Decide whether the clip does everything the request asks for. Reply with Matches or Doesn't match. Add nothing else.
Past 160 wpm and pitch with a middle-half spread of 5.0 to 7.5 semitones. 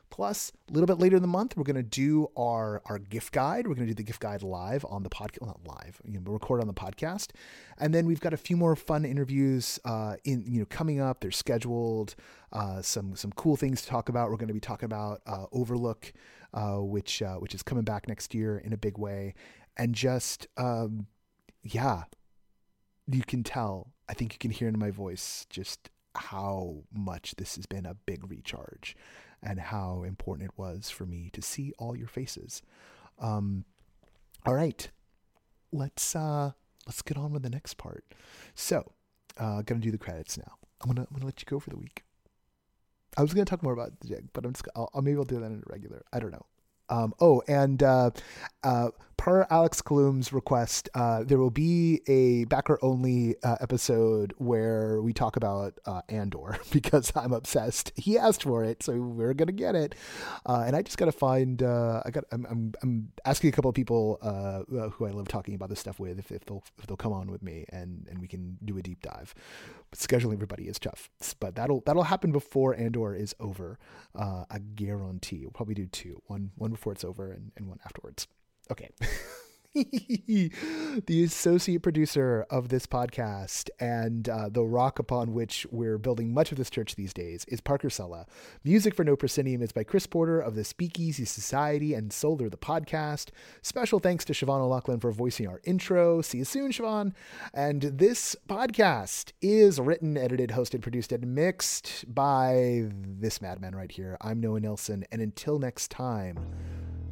Matches